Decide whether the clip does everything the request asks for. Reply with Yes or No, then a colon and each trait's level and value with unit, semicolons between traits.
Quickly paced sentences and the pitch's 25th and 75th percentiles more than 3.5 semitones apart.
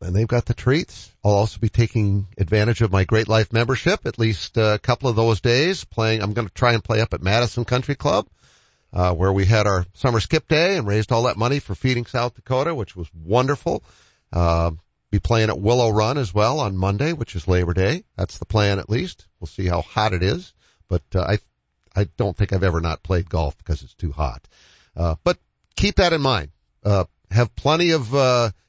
Yes: fast, 220 wpm; average, 4.5 semitones